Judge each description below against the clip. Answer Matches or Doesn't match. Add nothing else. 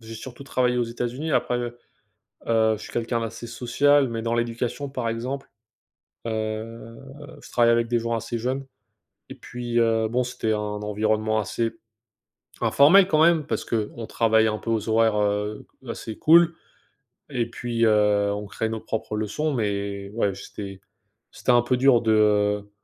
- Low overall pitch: Matches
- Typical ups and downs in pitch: Doesn't match